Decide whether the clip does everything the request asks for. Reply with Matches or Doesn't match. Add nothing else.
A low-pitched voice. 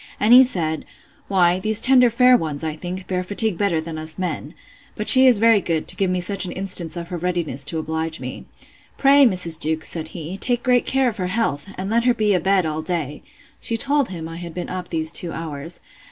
Doesn't match